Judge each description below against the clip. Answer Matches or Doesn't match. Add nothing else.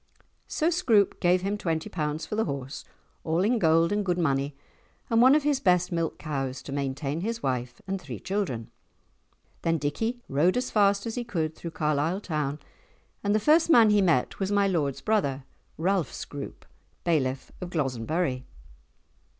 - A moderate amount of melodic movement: Doesn't match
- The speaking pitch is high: Doesn't match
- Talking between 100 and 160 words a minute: Doesn't match